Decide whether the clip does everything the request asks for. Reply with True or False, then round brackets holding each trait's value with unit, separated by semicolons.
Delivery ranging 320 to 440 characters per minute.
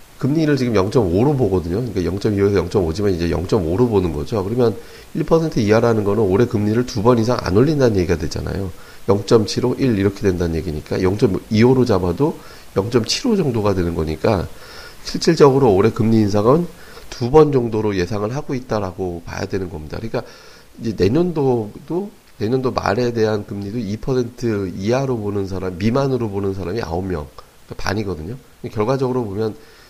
True (325 characters per minute)